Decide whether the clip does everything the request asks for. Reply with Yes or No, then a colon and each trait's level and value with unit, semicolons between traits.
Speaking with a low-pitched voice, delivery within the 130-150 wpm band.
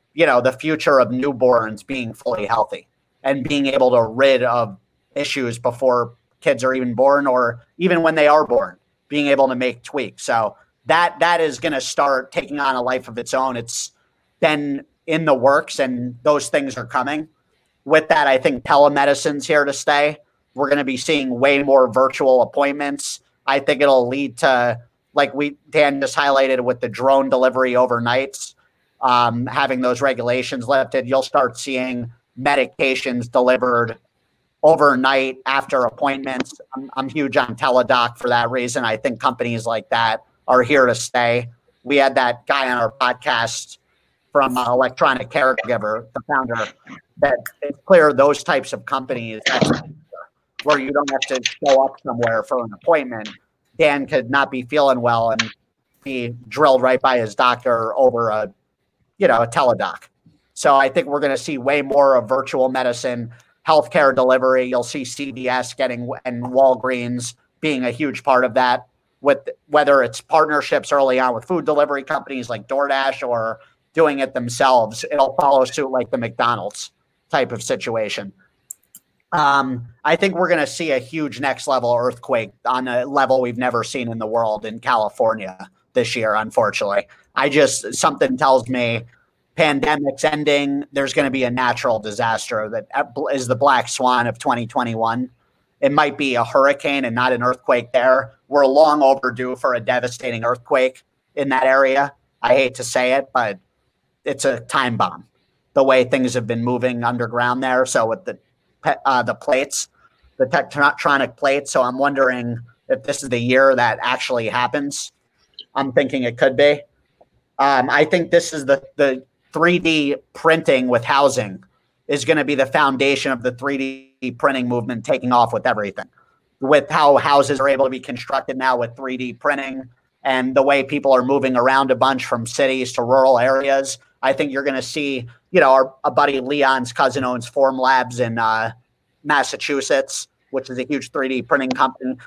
No: low, 130 Hz; average, 170 wpm